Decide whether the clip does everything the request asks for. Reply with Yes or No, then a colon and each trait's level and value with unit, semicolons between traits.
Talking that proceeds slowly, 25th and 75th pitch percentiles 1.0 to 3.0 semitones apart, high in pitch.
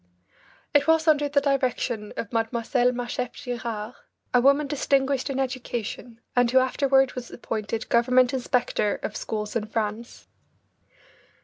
Yes: slow, 130 wpm; average, 2.7 semitones; very high, 250 Hz